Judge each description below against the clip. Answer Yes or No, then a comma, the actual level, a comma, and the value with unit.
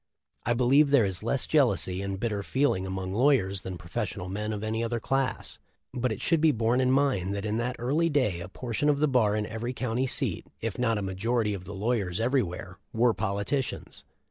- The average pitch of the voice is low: Yes, low, 115 Hz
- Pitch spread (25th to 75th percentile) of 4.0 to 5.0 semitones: Yes, average, 4.6 semitones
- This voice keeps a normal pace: No, fast, 215 wpm